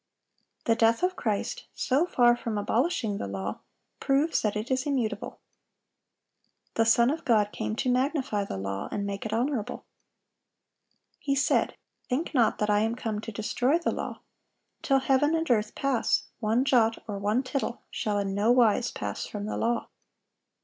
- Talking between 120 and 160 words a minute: No, average, 170 wpm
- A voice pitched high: Yes, high, 230 Hz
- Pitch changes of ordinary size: Yes, average, 4.2 semitones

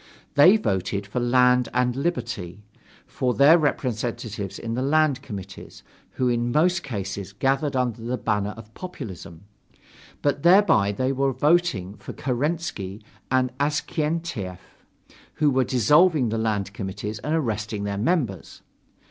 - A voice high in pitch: No, low, 125 Hz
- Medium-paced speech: No, slow, 130 wpm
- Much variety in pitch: Yes, wide, 5.9 semitones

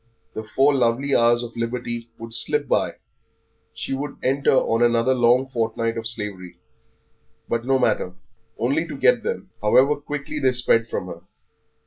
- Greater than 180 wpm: No, average, 155 wpm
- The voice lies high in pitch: No, low, 120 Hz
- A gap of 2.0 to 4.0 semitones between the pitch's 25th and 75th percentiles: Yes, average, 2.9 semitones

